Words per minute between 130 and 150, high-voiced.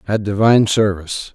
No: slow, 135 wpm; low, 105 Hz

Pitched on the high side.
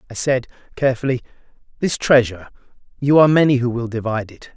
No: low, 125 Hz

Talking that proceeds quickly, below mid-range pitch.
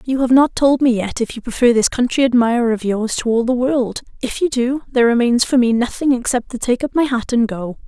No: fast, 260 wpm; high, 245 Hz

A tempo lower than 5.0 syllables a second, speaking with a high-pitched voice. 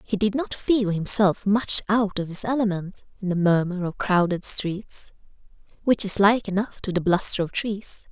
Yes: 4.5 syllables/s; high, 200 Hz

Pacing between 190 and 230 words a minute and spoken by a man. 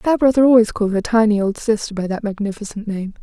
No: fast, 205 wpm; female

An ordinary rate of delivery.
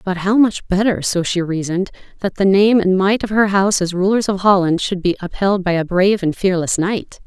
No: fast, 230 wpm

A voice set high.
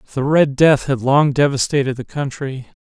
No: medium, 140 Hz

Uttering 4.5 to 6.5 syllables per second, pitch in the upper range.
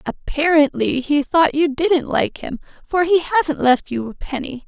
Yes: 4.6 syllables/s; very high, 300 Hz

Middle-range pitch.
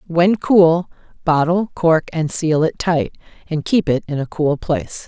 Yes: medium, 165 Hz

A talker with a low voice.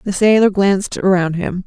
No: high, 190 Hz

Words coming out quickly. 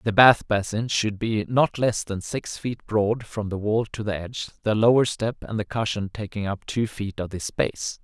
Yes: fast, 225 wpm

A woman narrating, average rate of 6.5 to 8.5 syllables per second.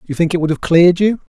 No: male; 6.9 syllables/s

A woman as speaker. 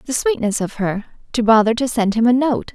Yes: female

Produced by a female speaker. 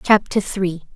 Yes: female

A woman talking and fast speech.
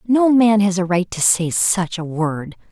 Yes: female; fast, 220 wpm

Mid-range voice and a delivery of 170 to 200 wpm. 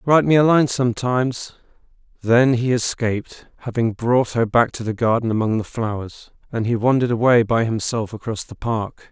No: low, 120 Hz; average, 180 wpm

